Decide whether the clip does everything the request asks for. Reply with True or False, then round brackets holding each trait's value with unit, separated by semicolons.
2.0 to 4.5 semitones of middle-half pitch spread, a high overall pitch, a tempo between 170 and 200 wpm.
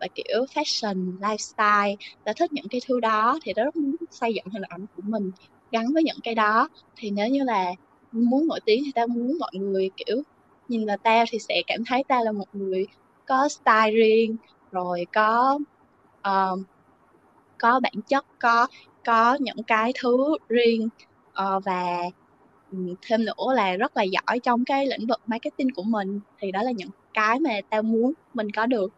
True (3.8 semitones; 225 Hz; 185 wpm)